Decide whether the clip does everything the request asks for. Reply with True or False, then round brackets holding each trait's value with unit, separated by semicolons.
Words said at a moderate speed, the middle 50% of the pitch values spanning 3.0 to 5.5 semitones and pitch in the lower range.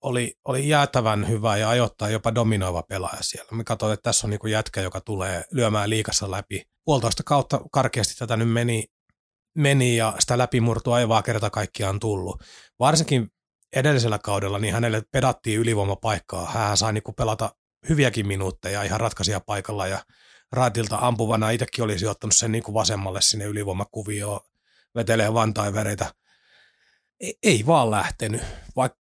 False (145 wpm; 2.5 semitones; 110 Hz)